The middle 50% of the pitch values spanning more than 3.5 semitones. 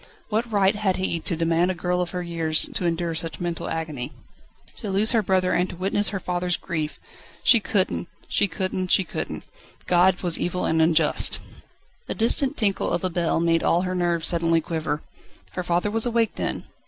No: narrow, 2.5 semitones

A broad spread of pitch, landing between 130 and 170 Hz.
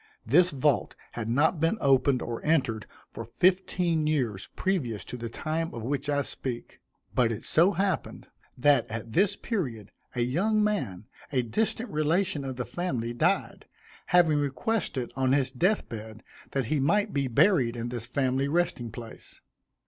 Yes: wide, 6.3 semitones; medium, 140 Hz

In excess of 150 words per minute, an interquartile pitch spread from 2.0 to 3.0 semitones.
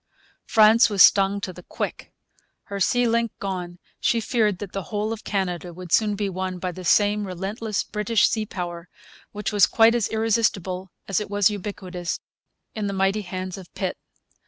Yes: average, 180 wpm; narrow, 2.6 semitones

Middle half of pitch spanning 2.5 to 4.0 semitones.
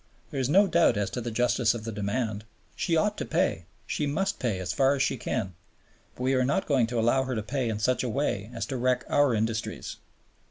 Yes: average, 3.7 semitones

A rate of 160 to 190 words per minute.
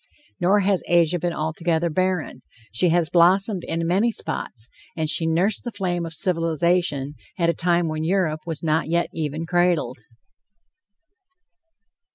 No: average, 145 wpm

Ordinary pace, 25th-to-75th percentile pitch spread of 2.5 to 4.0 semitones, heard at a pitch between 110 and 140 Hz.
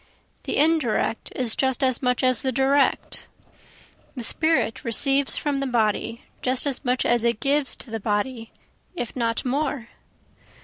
No: average, 150 wpm; average, 3.0 semitones; very high, 255 Hz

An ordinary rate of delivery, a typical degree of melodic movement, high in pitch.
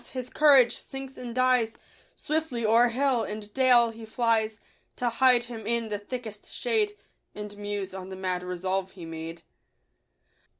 Yes: average, 155 wpm; average, 3.7 semitones; high, 230 Hz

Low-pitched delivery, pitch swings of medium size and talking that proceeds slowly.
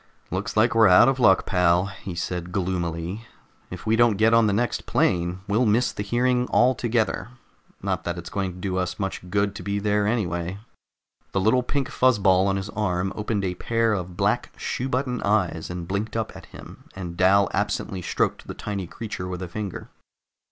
No: low, 100 Hz; average, 3.4 semitones; average, 195 wpm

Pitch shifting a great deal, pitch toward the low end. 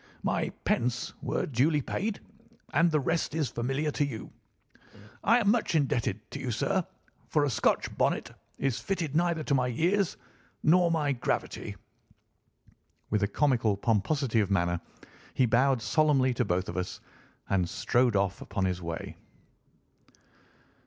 Yes: wide, 6.2 semitones; low, 130 Hz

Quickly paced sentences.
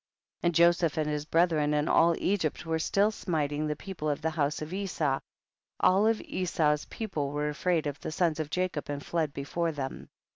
Yes: fast, 210 wpm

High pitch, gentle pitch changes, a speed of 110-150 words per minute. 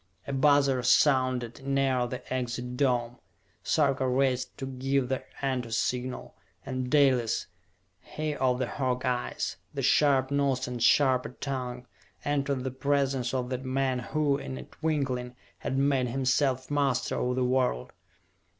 No: low, 130 Hz; narrow, 1.7 semitones; average, 140 wpm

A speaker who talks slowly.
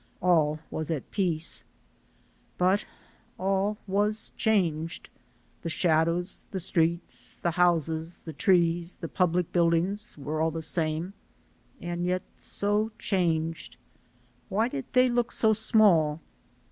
Yes: slow, 120 wpm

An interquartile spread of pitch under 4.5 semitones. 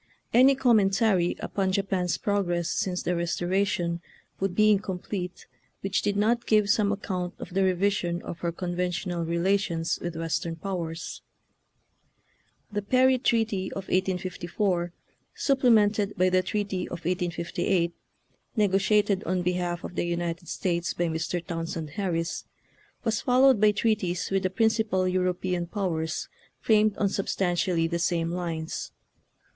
Yes: average, 2.9 semitones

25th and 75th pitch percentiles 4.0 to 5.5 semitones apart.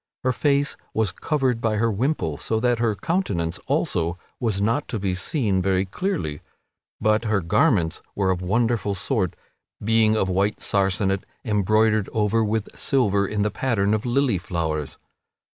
No: average, 3.5 semitones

